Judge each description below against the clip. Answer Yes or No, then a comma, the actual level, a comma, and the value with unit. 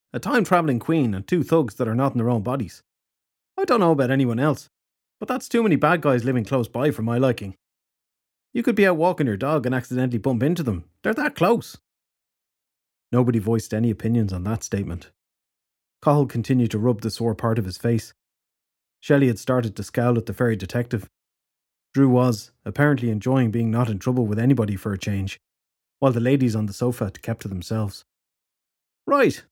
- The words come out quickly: No, average, 195 wpm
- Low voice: Yes, low, 120 Hz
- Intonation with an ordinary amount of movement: Yes, average, 4.1 semitones